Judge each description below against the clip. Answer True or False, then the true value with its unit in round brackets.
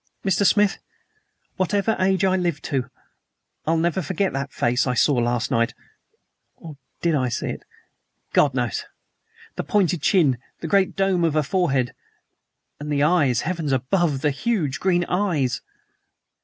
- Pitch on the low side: False (160 Hz)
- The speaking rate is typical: True (150 wpm)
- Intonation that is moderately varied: False (5.7 semitones)